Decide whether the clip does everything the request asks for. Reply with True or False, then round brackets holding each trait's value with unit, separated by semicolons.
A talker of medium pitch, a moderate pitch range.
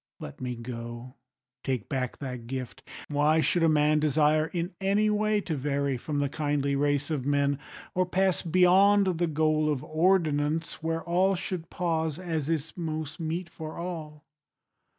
True (155 Hz; 3.3 semitones)